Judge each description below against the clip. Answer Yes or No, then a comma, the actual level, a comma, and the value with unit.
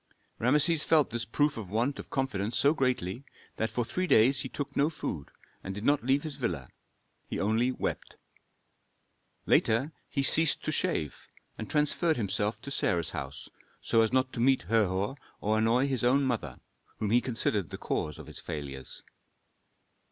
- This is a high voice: No, low, 120 Hz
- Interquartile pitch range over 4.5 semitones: Yes, average, 5.1 semitones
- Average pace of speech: Yes, average, 170 wpm